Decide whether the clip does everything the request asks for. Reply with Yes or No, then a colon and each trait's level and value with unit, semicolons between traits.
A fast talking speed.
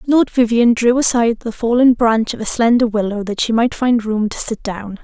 Yes: fast, 225 wpm